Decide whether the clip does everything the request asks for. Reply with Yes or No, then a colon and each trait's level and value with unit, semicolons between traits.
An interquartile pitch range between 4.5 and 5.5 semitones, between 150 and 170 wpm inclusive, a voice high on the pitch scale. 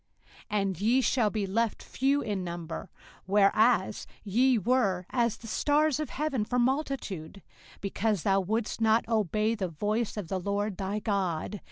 No: average, 3.5 semitones; average, 160 wpm; high, 210 Hz